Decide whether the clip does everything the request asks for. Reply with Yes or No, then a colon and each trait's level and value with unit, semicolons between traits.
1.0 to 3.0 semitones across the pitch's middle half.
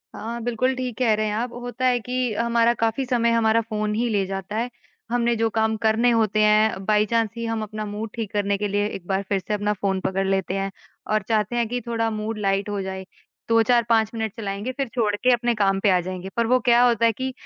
Yes: narrow, 2.5 semitones